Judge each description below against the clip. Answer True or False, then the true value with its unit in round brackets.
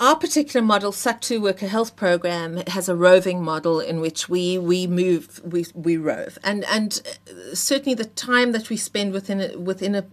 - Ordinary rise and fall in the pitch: True (3.9 semitones)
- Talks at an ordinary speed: True (185 wpm)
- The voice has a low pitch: False (190 Hz)